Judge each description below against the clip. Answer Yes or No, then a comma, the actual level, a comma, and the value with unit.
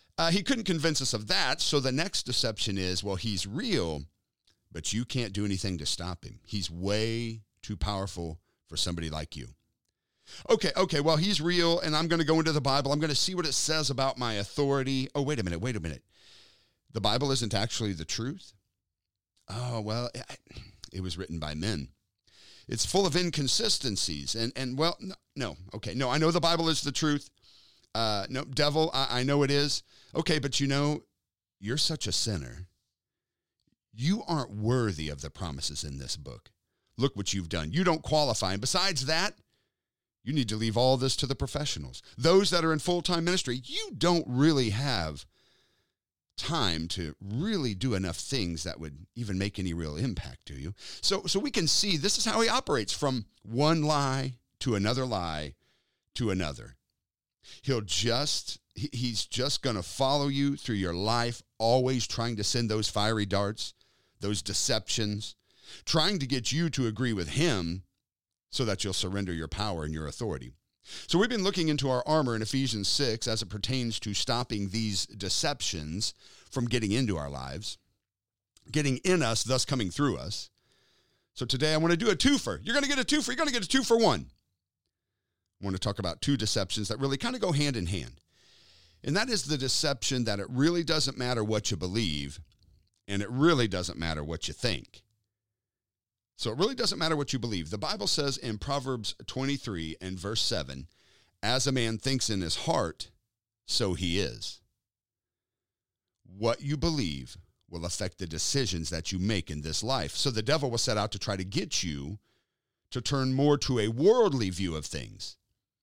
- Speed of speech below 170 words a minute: No, average, 185 wpm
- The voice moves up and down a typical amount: No, wide, 6.7 semitones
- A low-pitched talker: Yes, low, 115 Hz